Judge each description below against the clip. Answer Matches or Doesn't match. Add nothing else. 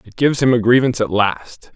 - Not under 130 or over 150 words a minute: Doesn't match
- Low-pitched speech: Matches